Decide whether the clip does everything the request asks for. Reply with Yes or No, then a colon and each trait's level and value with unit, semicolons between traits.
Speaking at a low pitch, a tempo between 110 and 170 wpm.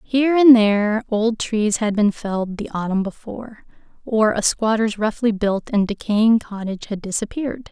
No: high, 215 Hz; average, 165 wpm